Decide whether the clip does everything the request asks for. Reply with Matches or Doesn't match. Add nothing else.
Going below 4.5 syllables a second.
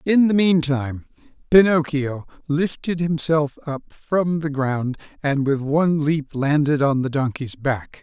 Matches